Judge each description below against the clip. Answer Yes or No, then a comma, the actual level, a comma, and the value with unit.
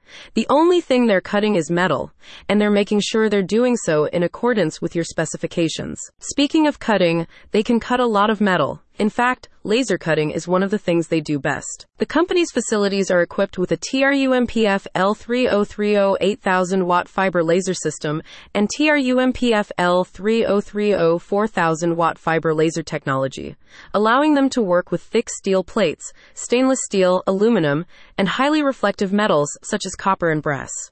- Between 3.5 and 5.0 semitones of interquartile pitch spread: Yes, average, 4.7 semitones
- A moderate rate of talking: Yes, average, 160 wpm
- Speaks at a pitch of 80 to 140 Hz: No, high, 200 Hz